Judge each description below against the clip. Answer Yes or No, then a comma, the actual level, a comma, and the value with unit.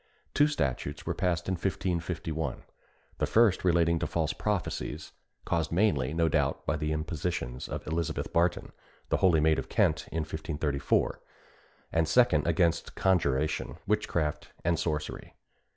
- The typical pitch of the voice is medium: No, very low, 80 Hz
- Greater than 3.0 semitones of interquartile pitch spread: No, narrow, 2.6 semitones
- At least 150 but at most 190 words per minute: No, average, 140 wpm